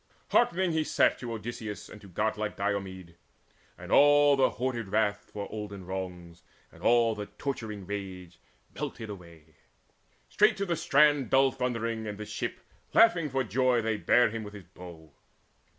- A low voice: Yes, low, 110 Hz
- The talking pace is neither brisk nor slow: Yes, average, 160 wpm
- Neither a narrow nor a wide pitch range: Yes, average, 4.8 semitones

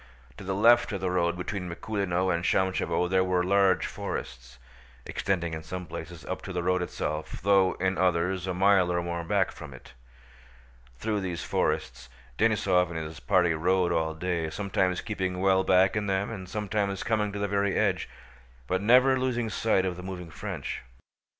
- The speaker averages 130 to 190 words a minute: Yes, average, 180 wpm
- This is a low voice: Yes, very low, 95 Hz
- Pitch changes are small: Yes, narrow, 2.3 semitones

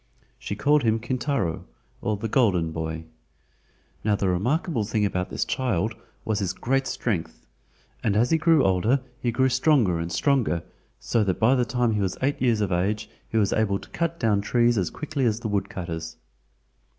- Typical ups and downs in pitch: Yes, average, 5.0 semitones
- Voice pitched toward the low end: Yes, low, 110 Hz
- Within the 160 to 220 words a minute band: Yes, average, 185 wpm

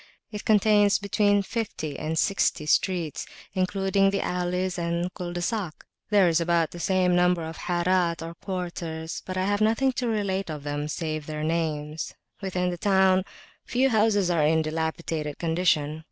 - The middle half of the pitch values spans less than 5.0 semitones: Yes, average, 3.4 semitones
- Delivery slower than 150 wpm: No, average, 170 wpm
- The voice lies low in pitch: No, medium, 180 Hz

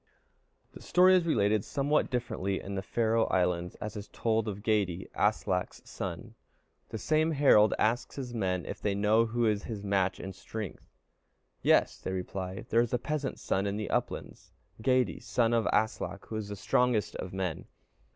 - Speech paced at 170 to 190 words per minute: Yes, average, 175 wpm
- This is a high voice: No, low, 110 Hz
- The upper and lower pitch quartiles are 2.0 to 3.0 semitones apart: No, average, 3.5 semitones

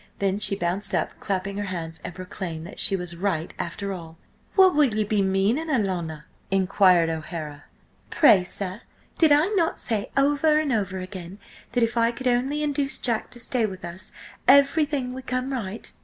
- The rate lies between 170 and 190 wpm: Yes, average, 180 wpm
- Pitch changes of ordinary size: No, wide, 6.2 semitones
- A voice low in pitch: No, high, 200 Hz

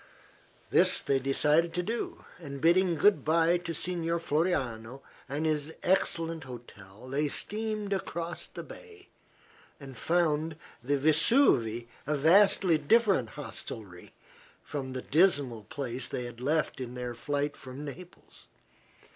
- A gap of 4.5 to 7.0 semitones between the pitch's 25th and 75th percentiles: Yes, average, 4.9 semitones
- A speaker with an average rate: No, slow, 130 wpm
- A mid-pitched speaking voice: Yes, medium, 150 Hz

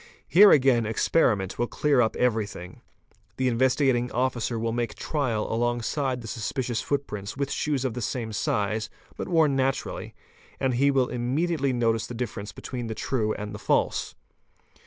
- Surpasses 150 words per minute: Yes, average, 160 wpm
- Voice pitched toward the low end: Yes, low, 120 Hz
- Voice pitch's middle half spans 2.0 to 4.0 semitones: Yes, average, 3.2 semitones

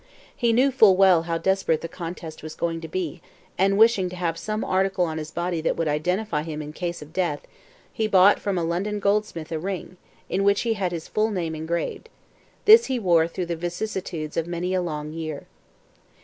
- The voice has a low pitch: No, medium, 175 Hz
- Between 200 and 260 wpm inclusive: Yes, fast, 205 wpm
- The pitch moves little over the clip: No, average, 3.3 semitones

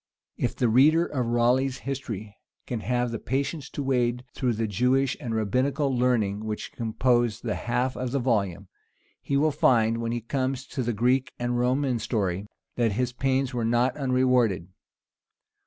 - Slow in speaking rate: No, average, 165 wpm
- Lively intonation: No, narrow, 2.5 semitones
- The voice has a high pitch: No, low, 125 Hz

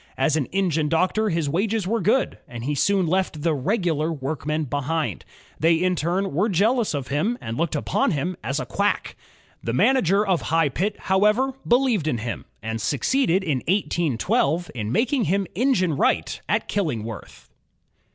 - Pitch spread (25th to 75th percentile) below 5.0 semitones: No, average, 5.3 semitones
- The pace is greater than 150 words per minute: Yes, average, 170 wpm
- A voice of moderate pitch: Yes, medium, 170 Hz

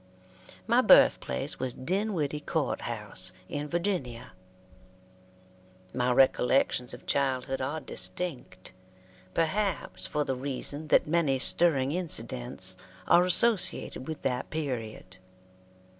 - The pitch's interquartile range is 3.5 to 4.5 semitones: No, average, 4.9 semitones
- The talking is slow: Yes, slow, 100 wpm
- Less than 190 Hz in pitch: Yes, medium, 140 Hz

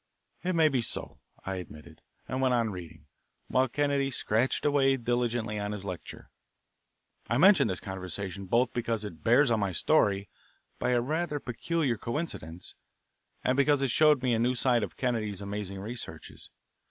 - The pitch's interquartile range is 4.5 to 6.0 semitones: Yes, average, 5.1 semitones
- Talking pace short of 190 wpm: Yes, average, 165 wpm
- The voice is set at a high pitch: No, low, 120 Hz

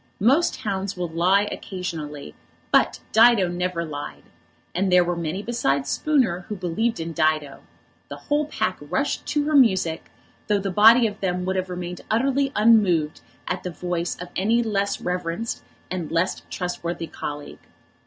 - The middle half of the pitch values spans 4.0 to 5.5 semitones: Yes, average, 4.5 semitones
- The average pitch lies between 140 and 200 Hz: Yes, medium, 185 Hz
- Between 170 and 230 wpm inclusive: No, average, 155 wpm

